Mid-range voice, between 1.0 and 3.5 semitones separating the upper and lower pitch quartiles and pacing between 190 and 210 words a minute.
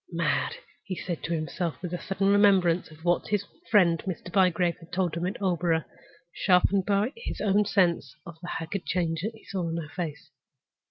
Yes: medium, 180 Hz; average, 2.8 semitones; average, 195 wpm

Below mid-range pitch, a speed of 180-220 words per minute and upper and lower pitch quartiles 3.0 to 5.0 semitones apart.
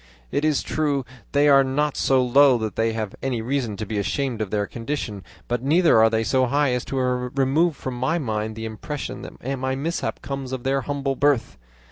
Yes: low, 130 Hz; fast, 205 wpm; average, 3.8 semitones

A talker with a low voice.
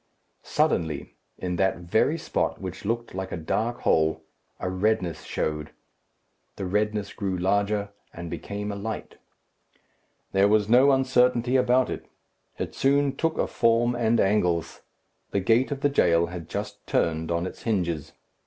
Yes: low, 100 Hz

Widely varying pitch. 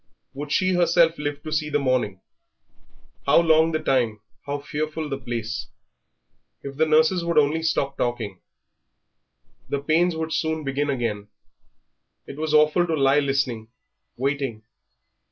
No: average, 2.9 semitones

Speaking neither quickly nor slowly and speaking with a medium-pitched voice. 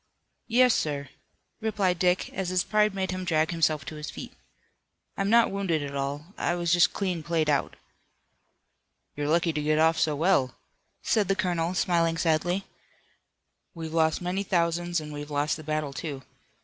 Yes: average, 170 wpm; medium, 165 Hz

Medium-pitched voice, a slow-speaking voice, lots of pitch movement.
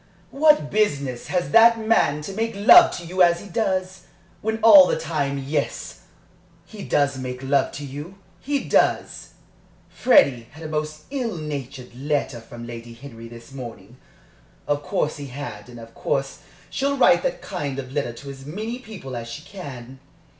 No: medium, 145 Hz; average, 170 wpm; wide, 6.9 semitones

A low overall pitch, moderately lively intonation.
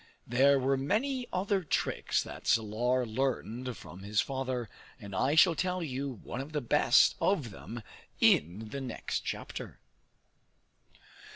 Yes: low, 130 Hz; average, 4.7 semitones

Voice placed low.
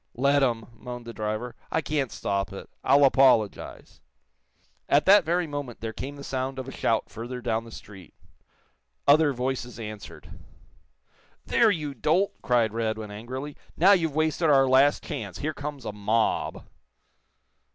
Yes: low, 130 Hz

